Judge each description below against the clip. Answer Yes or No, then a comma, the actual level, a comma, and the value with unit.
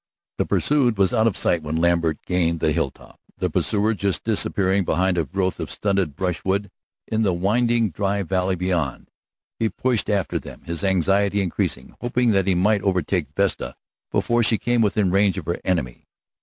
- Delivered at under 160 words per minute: No, average, 175 wpm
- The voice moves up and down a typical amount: Yes, average, 3.2 semitones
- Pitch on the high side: No, very low, 95 Hz